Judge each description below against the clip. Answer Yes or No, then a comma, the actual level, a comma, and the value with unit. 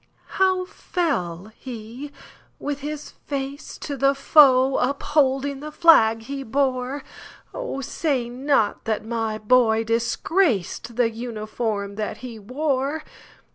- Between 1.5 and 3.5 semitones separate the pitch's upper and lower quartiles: No, average, 4.2 semitones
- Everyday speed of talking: No, slow, 95 wpm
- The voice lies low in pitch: No, very high, 260 Hz